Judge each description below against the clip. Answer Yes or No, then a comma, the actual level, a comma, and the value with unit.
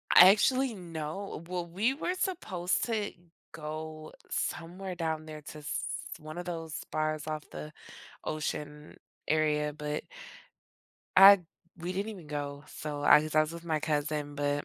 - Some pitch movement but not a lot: Yes, average, 3.1 semitones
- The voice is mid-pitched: Yes, medium, 155 Hz